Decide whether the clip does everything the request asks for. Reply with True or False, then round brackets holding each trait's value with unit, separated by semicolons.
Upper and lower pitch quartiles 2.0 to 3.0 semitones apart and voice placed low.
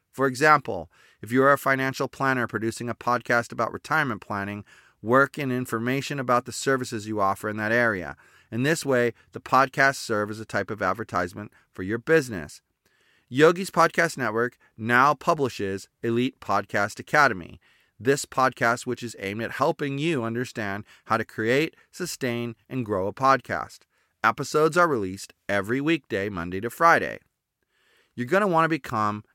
False (4.0 semitones; 120 Hz)